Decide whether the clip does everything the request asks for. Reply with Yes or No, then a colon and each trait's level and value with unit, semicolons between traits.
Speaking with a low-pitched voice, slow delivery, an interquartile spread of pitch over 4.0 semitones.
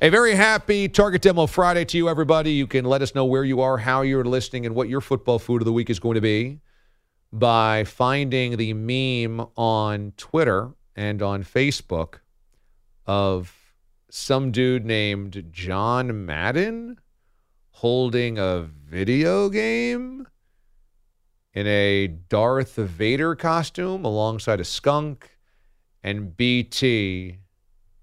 Yes: low, 120 Hz; slow, 130 wpm; average, 5.3 semitones